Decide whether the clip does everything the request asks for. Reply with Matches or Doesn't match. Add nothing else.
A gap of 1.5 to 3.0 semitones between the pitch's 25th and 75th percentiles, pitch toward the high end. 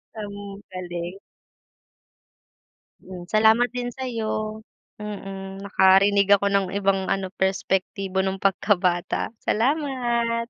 Matches